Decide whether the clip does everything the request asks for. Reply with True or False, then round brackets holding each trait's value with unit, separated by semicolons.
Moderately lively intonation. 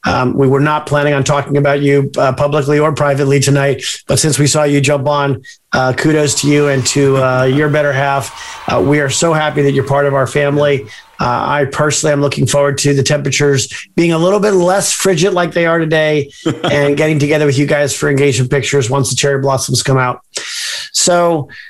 False (1.5 semitones)